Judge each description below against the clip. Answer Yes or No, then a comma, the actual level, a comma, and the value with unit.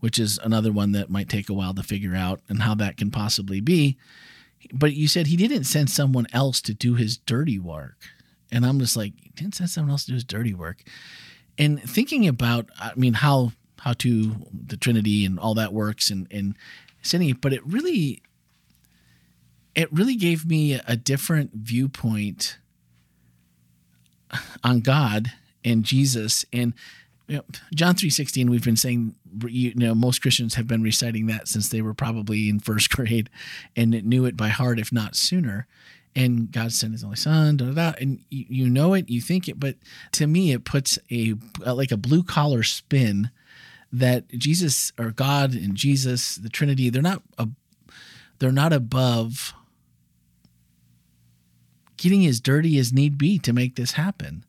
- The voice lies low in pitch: Yes, low, 120 Hz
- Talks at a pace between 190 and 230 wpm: No, average, 175 wpm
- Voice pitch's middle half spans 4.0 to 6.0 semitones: Yes, average, 4.8 semitones